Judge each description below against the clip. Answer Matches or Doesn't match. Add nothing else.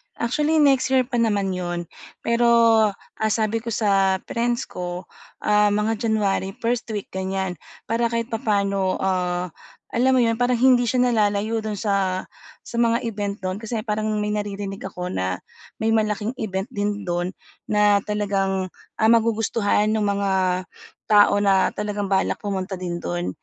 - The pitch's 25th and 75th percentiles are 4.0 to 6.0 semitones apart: Doesn't match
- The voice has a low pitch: Doesn't match